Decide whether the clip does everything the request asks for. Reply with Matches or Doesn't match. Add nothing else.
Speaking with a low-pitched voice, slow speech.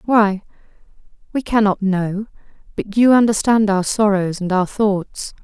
Doesn't match